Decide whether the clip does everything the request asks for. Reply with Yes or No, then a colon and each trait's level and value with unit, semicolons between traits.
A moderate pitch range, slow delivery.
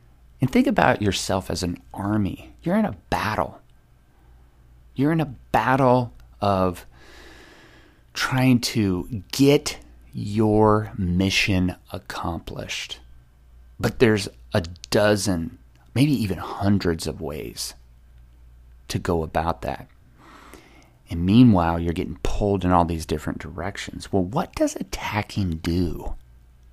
No: wide, 8.5 semitones; slow, 110 wpm